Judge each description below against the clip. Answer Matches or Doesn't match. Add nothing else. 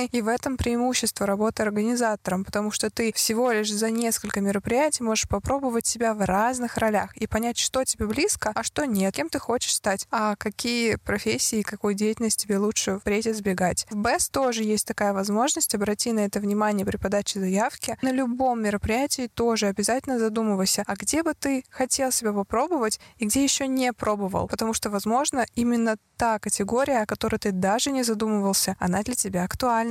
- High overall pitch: Matches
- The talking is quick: Matches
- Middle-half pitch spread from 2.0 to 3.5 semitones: Matches